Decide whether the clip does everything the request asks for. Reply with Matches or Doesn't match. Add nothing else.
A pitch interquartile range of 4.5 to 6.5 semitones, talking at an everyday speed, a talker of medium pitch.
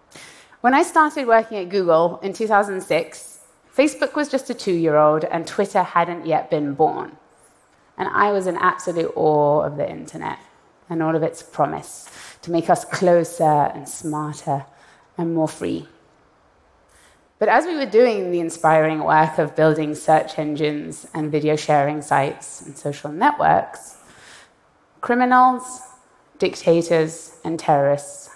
Matches